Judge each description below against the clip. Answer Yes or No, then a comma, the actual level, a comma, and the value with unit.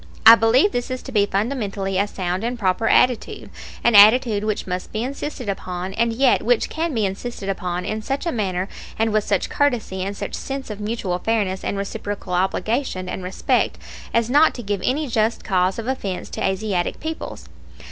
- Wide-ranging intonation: No, average, 4.1 semitones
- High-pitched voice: Yes, high, 215 Hz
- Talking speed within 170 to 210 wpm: Yes, average, 190 wpm